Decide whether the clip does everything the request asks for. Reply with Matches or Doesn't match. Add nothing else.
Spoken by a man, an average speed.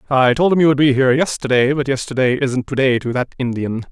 Doesn't match